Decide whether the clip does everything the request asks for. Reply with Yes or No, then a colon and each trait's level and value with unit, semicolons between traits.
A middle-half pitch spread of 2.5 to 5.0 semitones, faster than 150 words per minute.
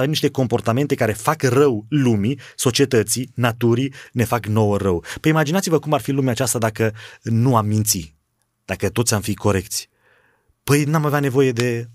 Yes: average, 4.0 semitones; average, 165 wpm